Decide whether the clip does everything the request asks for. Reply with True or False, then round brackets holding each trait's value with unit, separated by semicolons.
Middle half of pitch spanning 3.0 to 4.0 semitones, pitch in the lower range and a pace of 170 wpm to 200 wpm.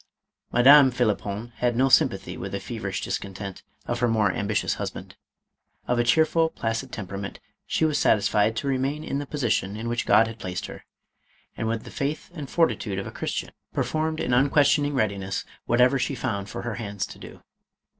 False (4.8 semitones; 120 Hz; 185 wpm)